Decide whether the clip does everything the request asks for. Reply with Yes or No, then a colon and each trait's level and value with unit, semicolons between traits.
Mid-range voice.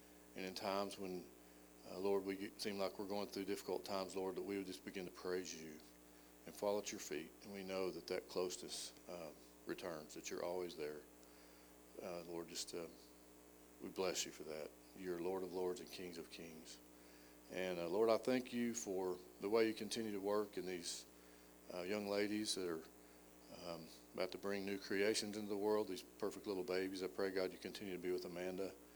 No: very low, 90 Hz